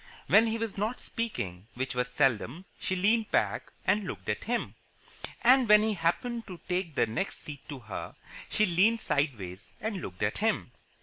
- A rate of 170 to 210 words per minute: Yes, average, 180 wpm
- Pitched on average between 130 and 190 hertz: Yes, medium, 185 Hz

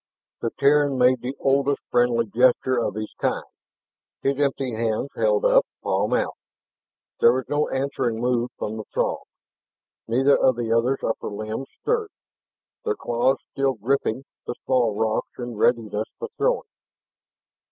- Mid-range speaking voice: No, low, 125 Hz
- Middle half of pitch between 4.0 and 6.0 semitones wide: No, average, 3.2 semitones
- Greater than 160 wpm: No, average, 145 wpm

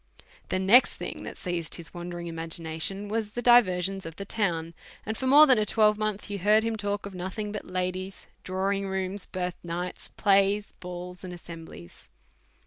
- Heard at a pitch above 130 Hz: Yes, high, 190 Hz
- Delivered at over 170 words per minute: Yes, average, 180 wpm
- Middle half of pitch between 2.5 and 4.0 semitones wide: Yes, average, 2.9 semitones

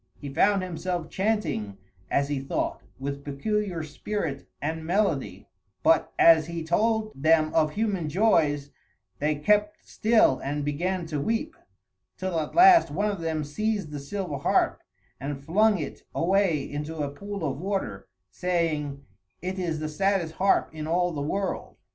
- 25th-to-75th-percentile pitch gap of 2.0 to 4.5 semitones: No, average, 5.2 semitones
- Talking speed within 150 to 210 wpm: Yes, average, 155 wpm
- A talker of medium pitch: Yes, medium, 165 Hz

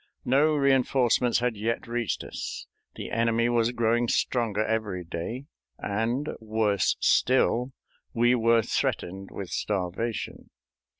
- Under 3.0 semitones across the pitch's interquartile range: Yes, narrow, 2.4 semitones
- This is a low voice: Yes, low, 115 Hz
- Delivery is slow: Yes, slow, 120 wpm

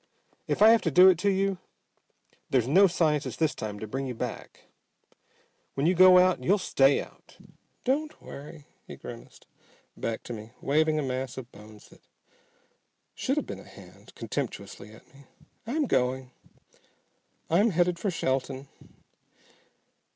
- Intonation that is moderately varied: No, wide, 6.1 semitones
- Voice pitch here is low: No, medium, 150 Hz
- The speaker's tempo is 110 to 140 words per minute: No, average, 150 wpm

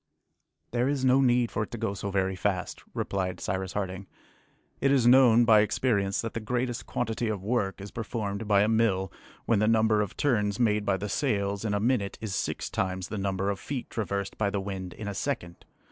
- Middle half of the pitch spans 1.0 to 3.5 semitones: Yes, average, 3.1 semitones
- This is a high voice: No, low, 105 Hz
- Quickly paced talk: Yes, fast, 210 wpm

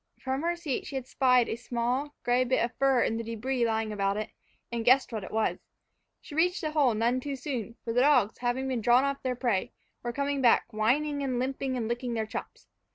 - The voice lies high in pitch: Yes, very high, 250 Hz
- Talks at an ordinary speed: No, fast, 225 wpm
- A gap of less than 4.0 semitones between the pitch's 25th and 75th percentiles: Yes, average, 2.8 semitones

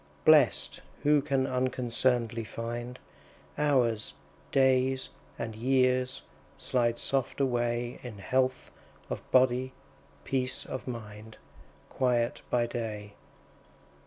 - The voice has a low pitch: Yes, low, 125 Hz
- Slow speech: Yes, slow, 95 wpm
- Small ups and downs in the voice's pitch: Yes, narrow, 1.8 semitones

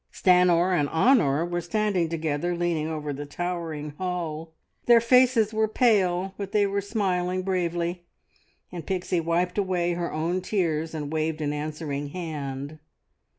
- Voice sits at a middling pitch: Yes, medium, 175 Hz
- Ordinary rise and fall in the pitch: Yes, average, 3.1 semitones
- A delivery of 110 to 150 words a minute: Yes, average, 145 wpm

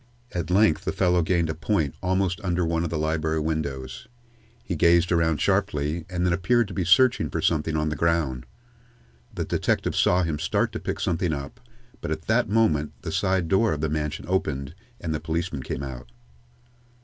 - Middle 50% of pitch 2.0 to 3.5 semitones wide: Yes, average, 2.9 semitones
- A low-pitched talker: Yes, very low, 80 Hz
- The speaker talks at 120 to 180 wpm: No, average, 190 wpm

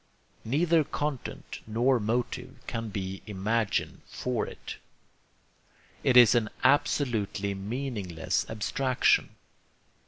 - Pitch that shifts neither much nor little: Yes, average, 4.0 semitones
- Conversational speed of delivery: No, slow, 90 wpm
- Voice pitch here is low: Yes, low, 115 Hz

